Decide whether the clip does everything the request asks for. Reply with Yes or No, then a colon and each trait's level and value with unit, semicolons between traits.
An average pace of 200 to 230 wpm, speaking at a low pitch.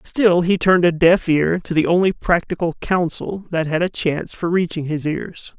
No: fast, 205 wpm; medium, 170 Hz